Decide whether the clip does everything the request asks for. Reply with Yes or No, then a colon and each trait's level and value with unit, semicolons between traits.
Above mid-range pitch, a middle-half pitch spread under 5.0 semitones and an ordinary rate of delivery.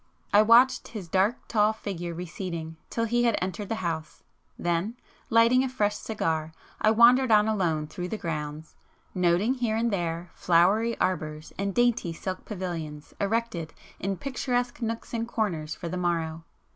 No: high, 195 Hz; wide, 5.4 semitones; average, 160 wpm